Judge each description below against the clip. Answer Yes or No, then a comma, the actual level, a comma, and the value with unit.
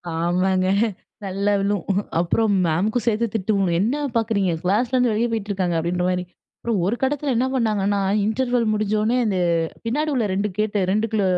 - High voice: Yes, high, 210 Hz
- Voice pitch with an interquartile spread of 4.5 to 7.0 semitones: No, average, 3.5 semitones